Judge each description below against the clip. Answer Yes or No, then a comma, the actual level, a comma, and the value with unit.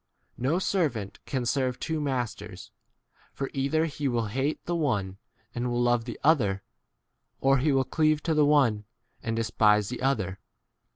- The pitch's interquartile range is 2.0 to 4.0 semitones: No, average, 4.6 semitones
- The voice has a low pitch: Yes, low, 130 Hz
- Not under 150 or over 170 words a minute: Yes, average, 160 wpm